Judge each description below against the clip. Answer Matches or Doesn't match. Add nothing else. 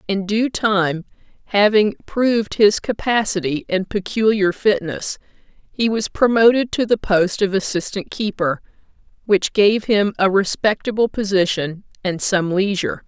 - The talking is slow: Matches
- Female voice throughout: Matches